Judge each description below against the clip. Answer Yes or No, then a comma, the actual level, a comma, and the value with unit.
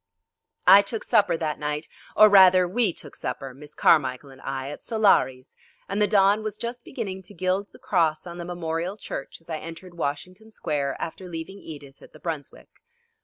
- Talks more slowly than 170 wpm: No, average, 185 wpm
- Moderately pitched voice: Yes, medium, 175 Hz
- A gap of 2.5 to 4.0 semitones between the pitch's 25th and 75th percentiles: No, average, 5.0 semitones